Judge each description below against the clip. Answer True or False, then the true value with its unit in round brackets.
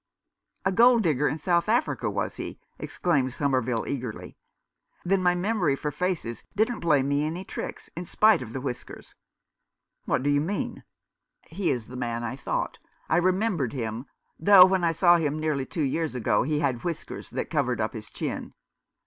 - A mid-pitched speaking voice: True (150 Hz)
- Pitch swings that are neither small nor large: False (5.7 semitones)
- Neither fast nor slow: True (190 wpm)